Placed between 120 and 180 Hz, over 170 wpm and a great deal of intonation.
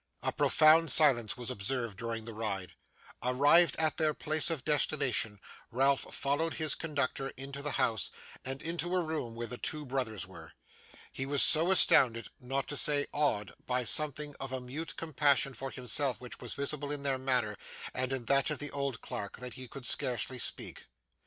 No: low, 135 Hz; average, 180 wpm; average, 3.2 semitones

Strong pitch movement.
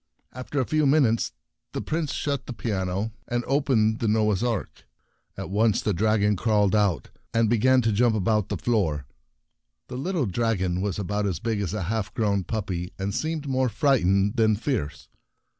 No: average, 3.8 semitones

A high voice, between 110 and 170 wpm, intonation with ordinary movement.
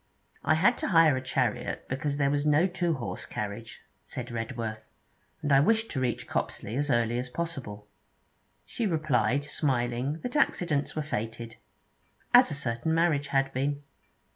No: medium, 140 Hz; average, 160 wpm; average, 4.7 semitones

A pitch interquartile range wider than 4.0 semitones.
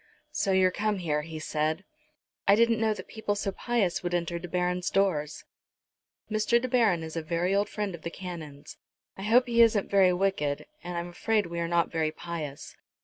No: average, 3.7 semitones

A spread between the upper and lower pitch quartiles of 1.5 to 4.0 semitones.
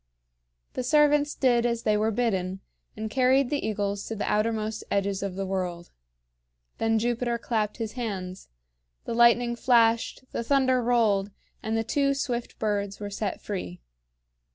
Yes: average, 3.2 semitones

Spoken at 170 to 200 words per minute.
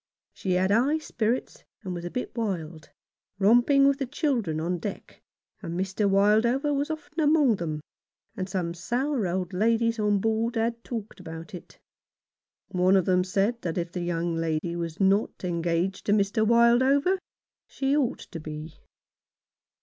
No: average, 155 wpm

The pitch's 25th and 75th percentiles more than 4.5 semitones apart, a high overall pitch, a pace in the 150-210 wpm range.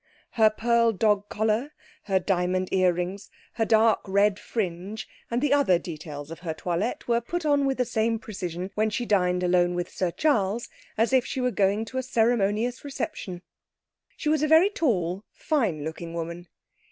Yes: average, 4.9 semitones; high, 210 Hz; average, 175 wpm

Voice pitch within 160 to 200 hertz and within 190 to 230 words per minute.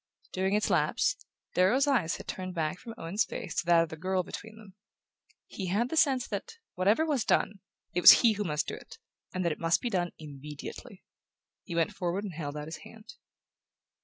Yes: medium, 185 Hz; fast, 205 wpm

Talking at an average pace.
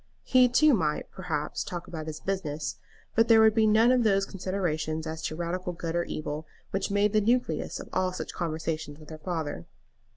Yes: average, 195 wpm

